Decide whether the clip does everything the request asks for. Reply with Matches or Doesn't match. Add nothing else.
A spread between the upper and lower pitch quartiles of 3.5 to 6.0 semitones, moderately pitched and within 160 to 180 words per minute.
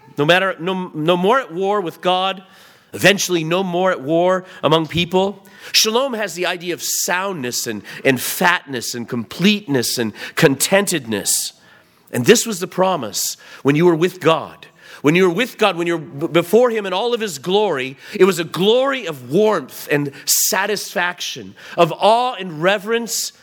Matches